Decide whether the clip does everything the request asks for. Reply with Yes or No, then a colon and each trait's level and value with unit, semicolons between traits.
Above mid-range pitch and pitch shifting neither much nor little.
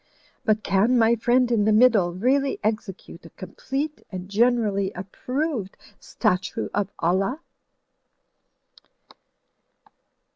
Yes: high, 215 Hz; average, 4.5 semitones